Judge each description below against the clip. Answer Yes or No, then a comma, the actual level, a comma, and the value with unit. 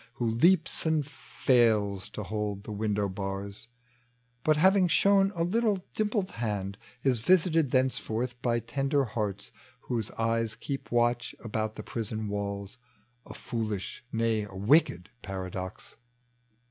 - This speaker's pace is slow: Yes, slow, 130 wpm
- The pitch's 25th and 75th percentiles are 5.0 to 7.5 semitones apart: Yes, wide, 5.6 semitones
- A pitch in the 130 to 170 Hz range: No, low, 115 Hz